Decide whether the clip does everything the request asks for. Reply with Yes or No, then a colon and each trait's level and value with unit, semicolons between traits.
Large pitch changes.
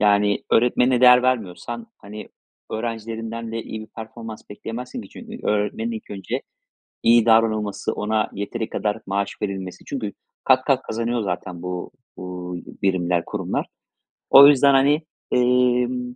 No: average, 3.3 semitones